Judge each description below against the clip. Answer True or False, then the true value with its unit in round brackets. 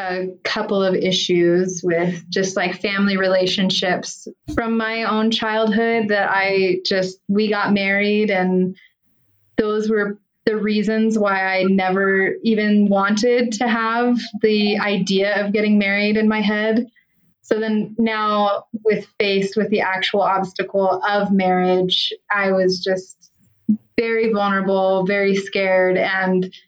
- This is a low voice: False (200 Hz)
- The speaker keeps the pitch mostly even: True (2.3 semitones)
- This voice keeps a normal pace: False (130 wpm)